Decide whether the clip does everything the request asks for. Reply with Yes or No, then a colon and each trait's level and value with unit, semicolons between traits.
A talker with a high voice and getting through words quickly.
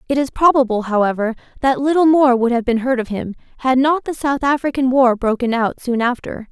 Yes: very high, 255 Hz; fast, 210 wpm